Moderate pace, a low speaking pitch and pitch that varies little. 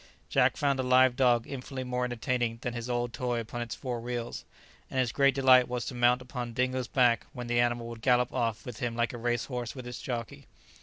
No: fast, 225 wpm; low, 125 Hz; narrow, 1.1 semitones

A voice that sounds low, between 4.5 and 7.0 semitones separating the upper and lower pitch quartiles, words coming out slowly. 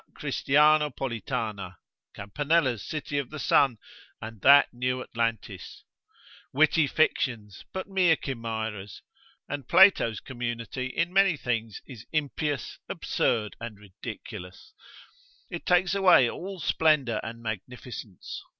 Yes: low, 125 Hz; average, 5.3 semitones; slow, 105 wpm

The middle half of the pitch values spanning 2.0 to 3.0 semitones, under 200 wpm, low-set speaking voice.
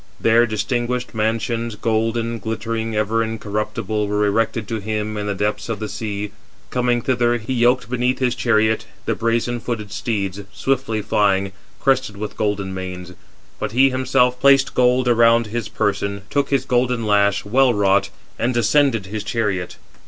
Yes: average, 2.7 semitones; average, 155 wpm; low, 115 Hz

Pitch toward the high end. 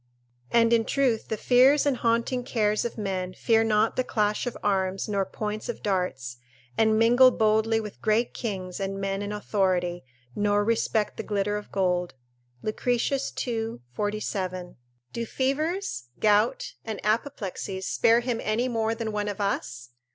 Yes: high, 215 Hz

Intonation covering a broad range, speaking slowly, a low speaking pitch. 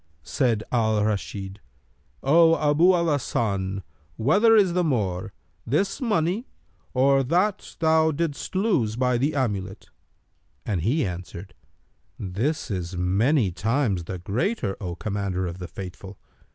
Yes: wide, 8.6 semitones; slow, 125 wpm; low, 115 Hz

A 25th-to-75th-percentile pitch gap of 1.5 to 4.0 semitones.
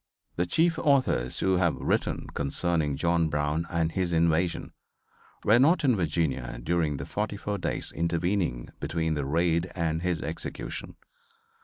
Yes: average, 2.8 semitones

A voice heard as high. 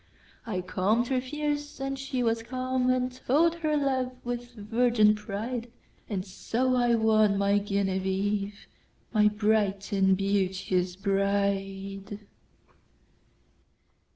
Yes: high, 215 Hz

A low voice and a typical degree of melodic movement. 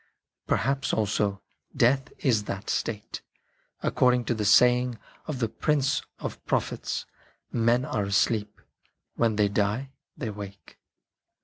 Yes: low, 115 Hz; average, 3.4 semitones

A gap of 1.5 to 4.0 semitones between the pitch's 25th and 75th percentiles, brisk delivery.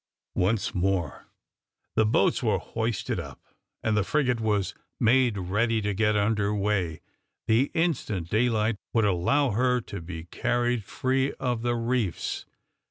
No: average, 3.3 semitones; average, 140 wpm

